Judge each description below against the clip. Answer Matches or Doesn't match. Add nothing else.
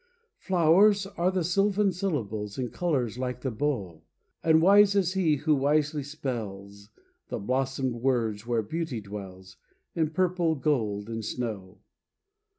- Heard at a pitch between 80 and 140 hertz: Matches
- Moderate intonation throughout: Doesn't match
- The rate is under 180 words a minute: Matches